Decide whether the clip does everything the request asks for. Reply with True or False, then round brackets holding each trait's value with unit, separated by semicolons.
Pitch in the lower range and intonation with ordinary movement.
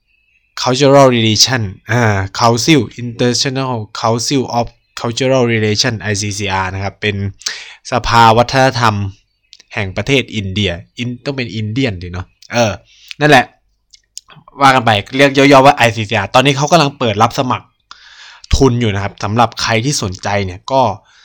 True (115 Hz; 3.9 semitones)